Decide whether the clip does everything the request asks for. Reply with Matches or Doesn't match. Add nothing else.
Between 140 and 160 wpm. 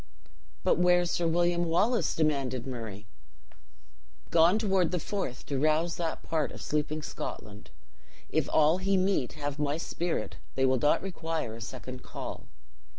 Matches